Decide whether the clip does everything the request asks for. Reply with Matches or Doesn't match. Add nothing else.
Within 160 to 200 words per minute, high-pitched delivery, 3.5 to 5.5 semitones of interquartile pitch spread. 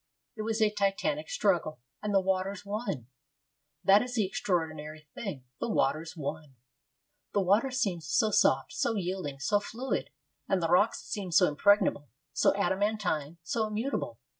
Doesn't match